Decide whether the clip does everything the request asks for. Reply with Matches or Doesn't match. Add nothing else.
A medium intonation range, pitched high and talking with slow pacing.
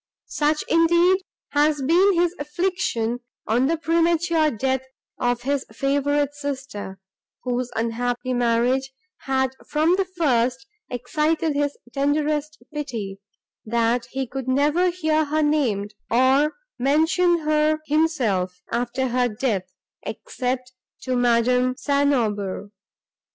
Matches